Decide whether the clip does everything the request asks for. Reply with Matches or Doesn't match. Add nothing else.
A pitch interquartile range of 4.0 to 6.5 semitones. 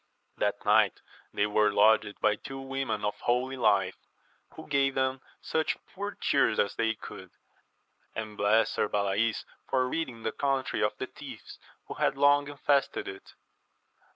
Matches